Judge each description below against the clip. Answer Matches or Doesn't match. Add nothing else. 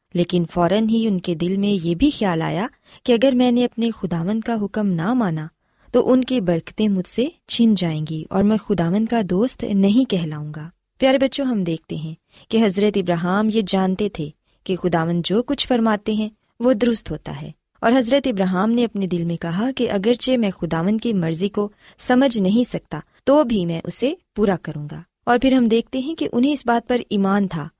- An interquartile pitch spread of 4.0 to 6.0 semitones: Matches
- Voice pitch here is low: Doesn't match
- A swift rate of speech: Matches